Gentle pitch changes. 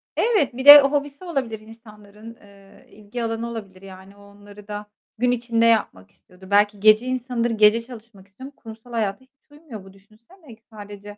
No: average, 3.3 semitones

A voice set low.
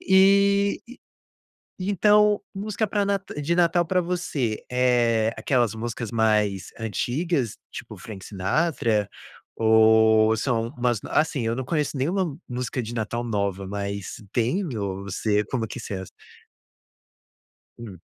Yes: low, 120 Hz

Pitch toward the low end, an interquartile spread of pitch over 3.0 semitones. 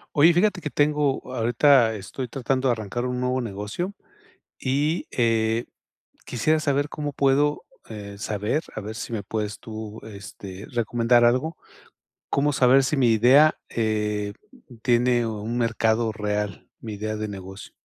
Yes: low, 120 Hz; average, 4.1 semitones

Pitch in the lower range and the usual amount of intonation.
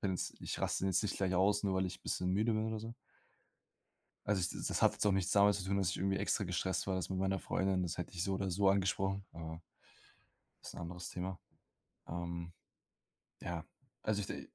No: very low, 95 Hz; narrow, 1.7 semitones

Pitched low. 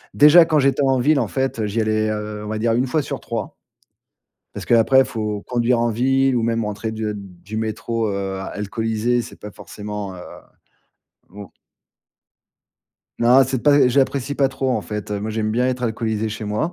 Yes: low, 115 Hz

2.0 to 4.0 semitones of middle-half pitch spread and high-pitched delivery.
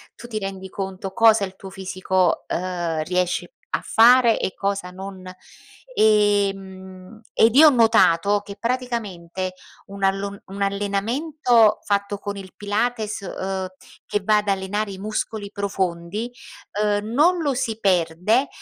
Yes: narrow, 2.5 semitones; high, 200 Hz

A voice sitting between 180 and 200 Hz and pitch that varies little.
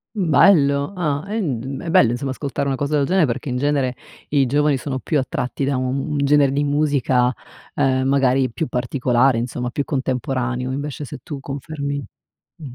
No: medium, 140 Hz; narrow, 2.1 semitones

